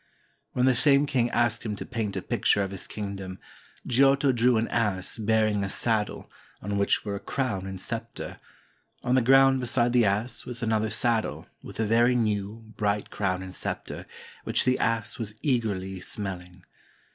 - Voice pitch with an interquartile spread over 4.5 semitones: No, average, 3.4 semitones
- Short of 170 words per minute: No, average, 175 wpm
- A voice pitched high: No, low, 110 Hz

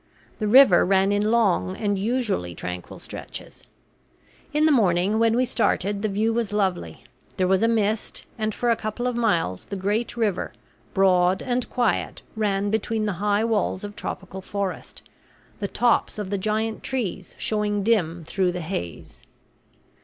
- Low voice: No, high, 205 Hz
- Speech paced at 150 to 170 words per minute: Yes, average, 160 wpm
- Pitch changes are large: No, average, 3.0 semitones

